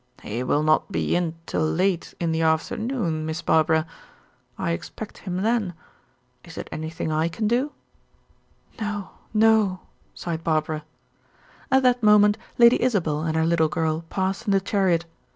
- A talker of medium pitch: Yes, medium, 175 Hz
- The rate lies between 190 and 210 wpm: No, average, 150 wpm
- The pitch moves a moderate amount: Yes, average, 4.8 semitones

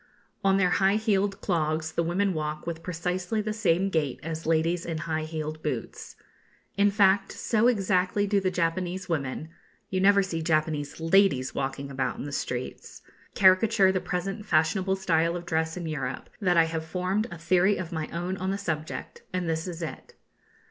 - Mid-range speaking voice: Yes, medium, 175 Hz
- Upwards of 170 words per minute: Yes, average, 180 wpm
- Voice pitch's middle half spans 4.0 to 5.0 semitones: No, average, 3.3 semitones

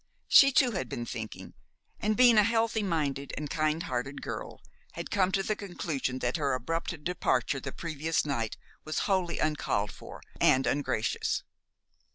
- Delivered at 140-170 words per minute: Yes, average, 160 wpm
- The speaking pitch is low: No, medium, 155 Hz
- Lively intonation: Yes, wide, 6.4 semitones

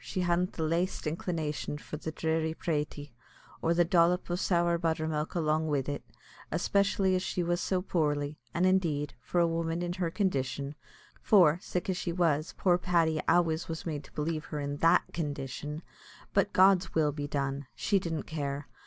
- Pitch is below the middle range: No, medium, 165 Hz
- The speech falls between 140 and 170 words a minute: No, average, 180 wpm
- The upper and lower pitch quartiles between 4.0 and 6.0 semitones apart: No, average, 2.8 semitones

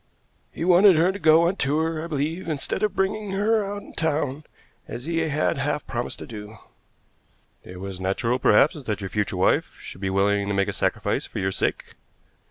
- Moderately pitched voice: Yes, medium, 145 Hz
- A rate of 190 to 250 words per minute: Yes, average, 195 wpm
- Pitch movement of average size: No, wide, 8.4 semitones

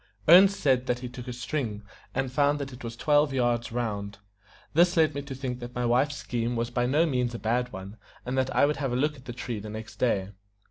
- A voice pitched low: Yes, low, 125 Hz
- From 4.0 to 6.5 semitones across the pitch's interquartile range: No, average, 3.2 semitones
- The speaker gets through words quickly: Yes, fast, 245 wpm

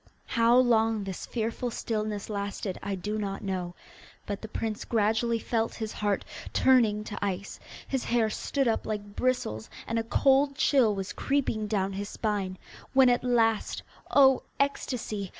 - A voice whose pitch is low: No, high, 220 Hz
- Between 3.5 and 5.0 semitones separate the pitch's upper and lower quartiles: No, average, 3.0 semitones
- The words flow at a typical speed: Yes, average, 155 wpm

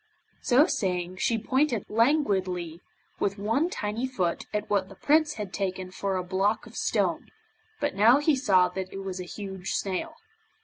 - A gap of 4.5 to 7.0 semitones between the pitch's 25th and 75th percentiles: Yes, average, 5.2 semitones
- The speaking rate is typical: Yes, average, 170 wpm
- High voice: Yes, high, 200 Hz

